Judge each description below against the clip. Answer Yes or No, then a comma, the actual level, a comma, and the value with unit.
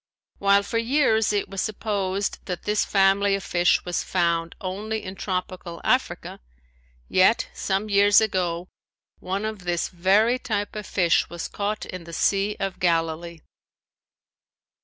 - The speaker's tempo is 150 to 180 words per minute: No, average, 140 wpm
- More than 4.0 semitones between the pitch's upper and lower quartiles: No, average, 2.9 semitones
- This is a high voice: Yes, high, 195 Hz